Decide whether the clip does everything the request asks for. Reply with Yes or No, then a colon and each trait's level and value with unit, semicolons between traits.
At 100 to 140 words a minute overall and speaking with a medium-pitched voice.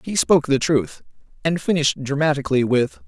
No: average, 155 wpm; medium, 145 Hz